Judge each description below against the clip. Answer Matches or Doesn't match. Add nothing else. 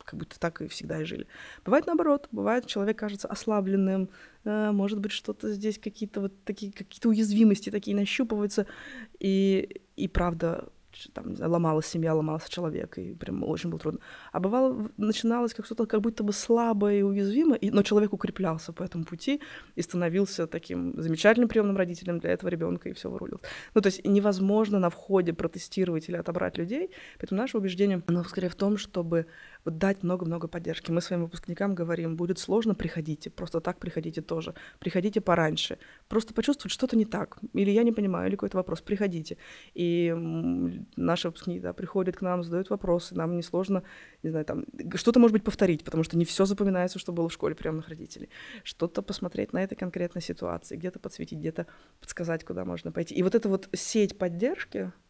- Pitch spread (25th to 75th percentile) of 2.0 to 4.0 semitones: Matches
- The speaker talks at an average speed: Doesn't match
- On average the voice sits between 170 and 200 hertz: Matches